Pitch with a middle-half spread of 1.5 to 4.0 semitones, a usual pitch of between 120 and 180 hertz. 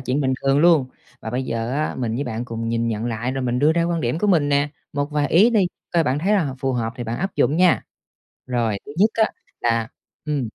No: average, 5.3 semitones; low, 135 Hz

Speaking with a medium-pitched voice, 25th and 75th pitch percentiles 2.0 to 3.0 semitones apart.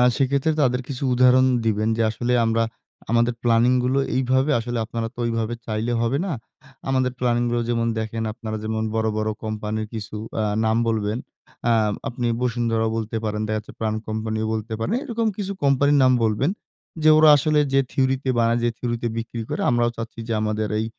No: low, 115 Hz; narrow, 2.5 semitones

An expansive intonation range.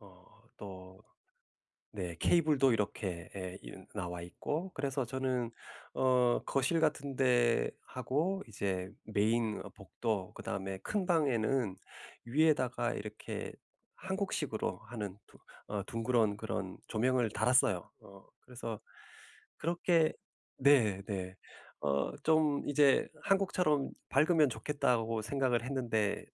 Yes: wide, 5.7 semitones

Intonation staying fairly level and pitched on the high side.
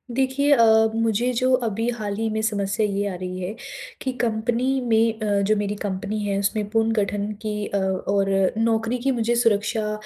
Yes: narrow, 2.0 semitones; high, 220 Hz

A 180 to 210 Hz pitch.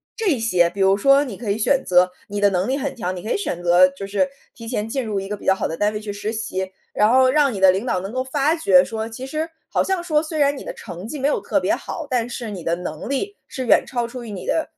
No: high, 225 Hz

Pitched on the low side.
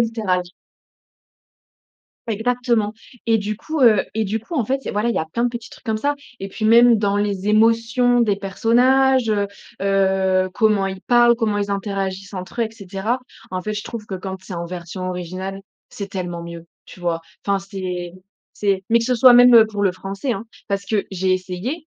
No: high, 205 Hz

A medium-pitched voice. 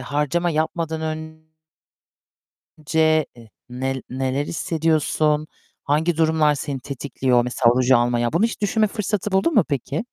Yes: medium, 155 Hz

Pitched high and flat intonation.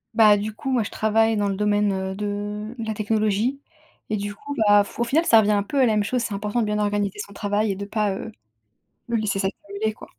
Yes: high, 210 Hz; narrow, 1.4 semitones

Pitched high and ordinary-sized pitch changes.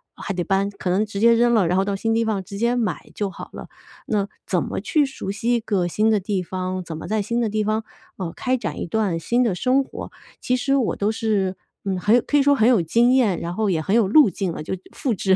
Yes: high, 210 Hz; average, 3.8 semitones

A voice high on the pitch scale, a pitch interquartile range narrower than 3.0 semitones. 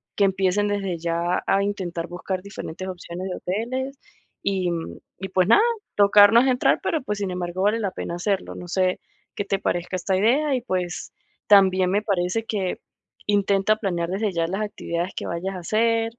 Yes: high, 195 Hz; narrow, 2.5 semitones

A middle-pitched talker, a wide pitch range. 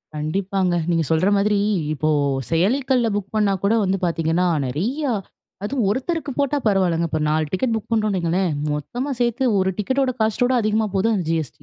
No: high, 200 Hz; wide, 5.8 semitones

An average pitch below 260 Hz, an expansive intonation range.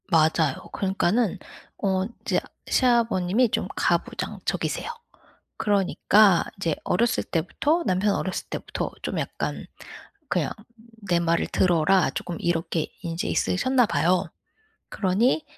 No: high, 190 Hz; average, 4.3 semitones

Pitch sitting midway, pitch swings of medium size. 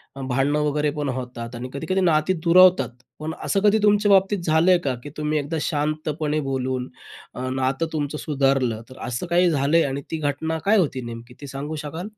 Yes: medium, 150 Hz; average, 3.8 semitones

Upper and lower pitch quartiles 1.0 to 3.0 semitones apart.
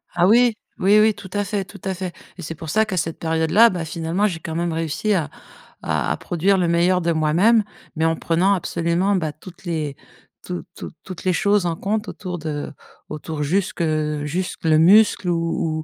No: average, 3.4 semitones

